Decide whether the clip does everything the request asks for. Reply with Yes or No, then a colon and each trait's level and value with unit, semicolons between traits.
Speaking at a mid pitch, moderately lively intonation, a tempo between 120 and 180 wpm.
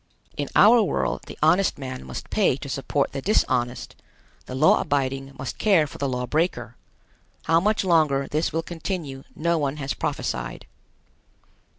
Yes: medium, 145 Hz; average, 4.0 semitones; average, 160 wpm